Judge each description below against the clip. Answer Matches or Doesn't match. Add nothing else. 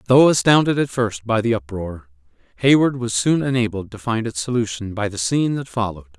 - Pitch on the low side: Matches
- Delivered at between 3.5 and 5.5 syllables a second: Doesn't match